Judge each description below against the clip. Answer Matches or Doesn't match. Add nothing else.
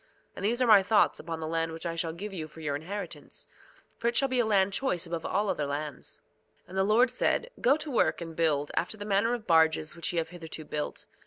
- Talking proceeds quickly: Matches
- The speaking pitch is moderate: Matches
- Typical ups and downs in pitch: Matches